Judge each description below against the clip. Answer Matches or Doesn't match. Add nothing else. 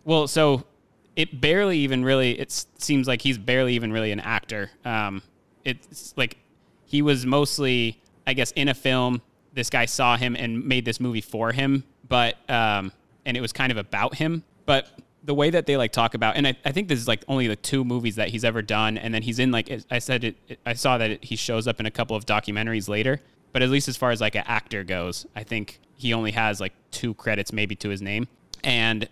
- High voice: Doesn't match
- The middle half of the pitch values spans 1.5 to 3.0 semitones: Doesn't match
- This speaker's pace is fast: Matches